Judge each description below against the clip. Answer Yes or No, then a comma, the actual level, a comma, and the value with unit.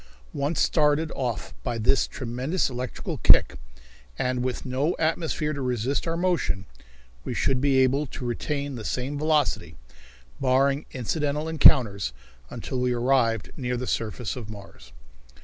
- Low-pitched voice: Yes, low, 130 Hz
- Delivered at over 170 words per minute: No, average, 140 wpm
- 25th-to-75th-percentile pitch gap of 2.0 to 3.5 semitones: Yes, average, 3.2 semitones